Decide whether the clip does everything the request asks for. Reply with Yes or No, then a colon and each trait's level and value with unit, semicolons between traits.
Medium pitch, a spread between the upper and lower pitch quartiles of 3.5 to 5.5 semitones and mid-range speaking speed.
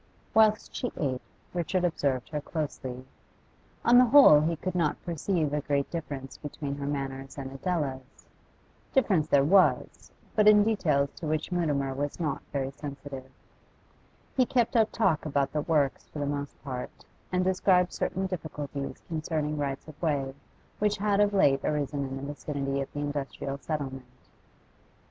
Yes: medium, 150 Hz; average, 4.5 semitones; average, 160 wpm